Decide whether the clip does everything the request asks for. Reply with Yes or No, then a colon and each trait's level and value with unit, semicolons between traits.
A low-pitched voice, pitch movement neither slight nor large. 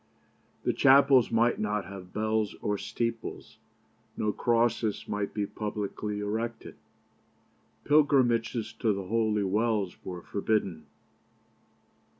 No: low, 110 Hz; narrow, 2.2 semitones